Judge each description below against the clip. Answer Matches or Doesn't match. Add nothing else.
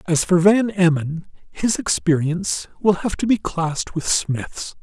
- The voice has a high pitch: Doesn't match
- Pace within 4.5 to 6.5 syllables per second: Doesn't match